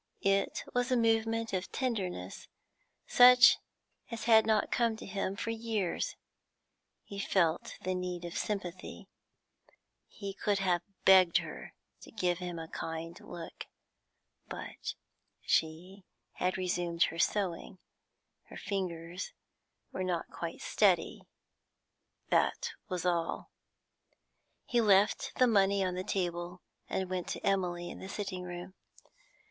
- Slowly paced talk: Yes, slow, 125 wpm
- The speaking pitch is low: No, high, 190 Hz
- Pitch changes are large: No, average, 3.2 semitones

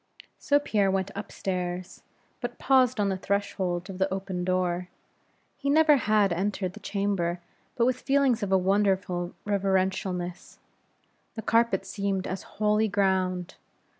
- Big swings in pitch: No, narrow, 2.5 semitones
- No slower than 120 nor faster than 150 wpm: Yes, average, 140 wpm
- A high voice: Yes, high, 195 Hz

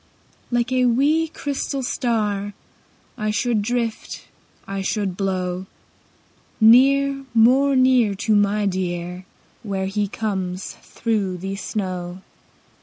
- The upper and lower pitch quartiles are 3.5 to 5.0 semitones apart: Yes, average, 4.4 semitones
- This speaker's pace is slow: Yes, slow, 110 wpm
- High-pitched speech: Yes, high, 210 Hz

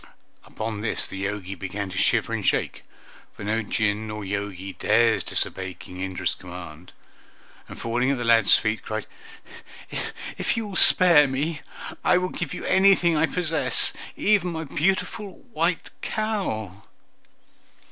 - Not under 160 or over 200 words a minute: No, average, 145 wpm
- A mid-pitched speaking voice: No, low, 115 Hz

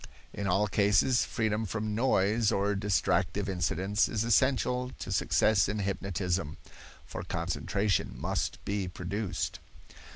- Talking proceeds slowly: Yes, slow, 120 wpm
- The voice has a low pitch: Yes, low, 100 Hz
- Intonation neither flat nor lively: No, narrow, 2.1 semitones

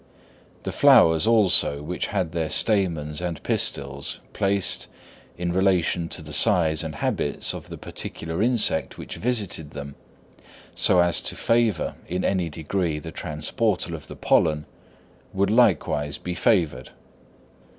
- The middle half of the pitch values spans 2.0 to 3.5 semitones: No, average, 4.2 semitones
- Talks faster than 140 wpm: No, slow, 135 wpm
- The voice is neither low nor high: No, very low, 85 Hz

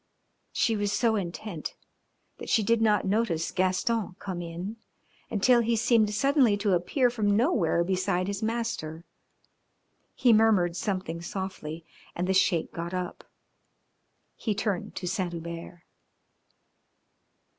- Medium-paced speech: No, slow, 125 wpm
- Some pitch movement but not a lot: Yes, average, 4.1 semitones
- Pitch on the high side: Yes, high, 195 Hz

